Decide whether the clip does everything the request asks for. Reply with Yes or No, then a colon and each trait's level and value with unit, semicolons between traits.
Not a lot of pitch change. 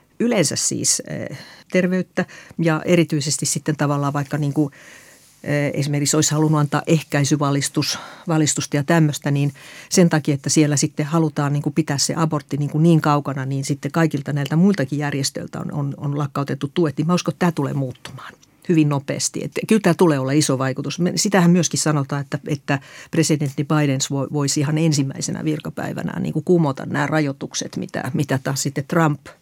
Yes: narrow, 2.3 semitones